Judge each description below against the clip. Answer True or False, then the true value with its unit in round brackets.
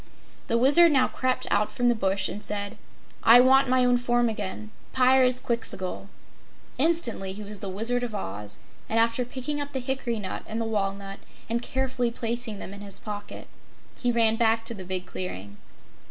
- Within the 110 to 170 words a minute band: False (180 wpm)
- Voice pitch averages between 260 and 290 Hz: False (230 Hz)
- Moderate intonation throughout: True (3.9 semitones)